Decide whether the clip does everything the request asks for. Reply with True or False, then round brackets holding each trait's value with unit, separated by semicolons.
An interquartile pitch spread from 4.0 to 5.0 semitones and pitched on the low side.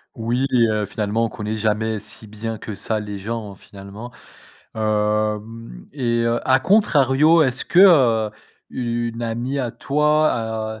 False (2.7 semitones; 115 Hz)